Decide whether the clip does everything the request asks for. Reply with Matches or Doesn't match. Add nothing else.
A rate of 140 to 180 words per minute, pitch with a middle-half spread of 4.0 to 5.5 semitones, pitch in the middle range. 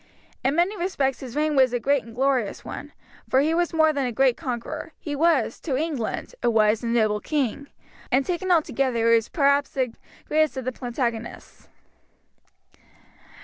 Doesn't match